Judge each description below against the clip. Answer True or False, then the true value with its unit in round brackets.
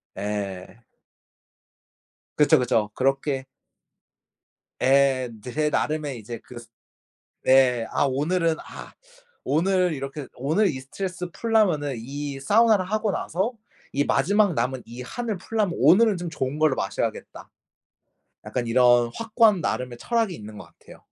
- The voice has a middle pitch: True (145 Hz)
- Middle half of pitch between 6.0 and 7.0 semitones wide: True (6.5 semitones)